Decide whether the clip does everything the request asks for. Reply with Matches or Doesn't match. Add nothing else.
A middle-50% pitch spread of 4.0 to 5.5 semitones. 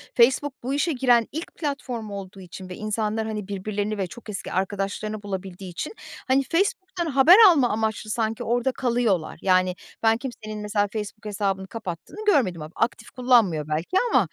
Matches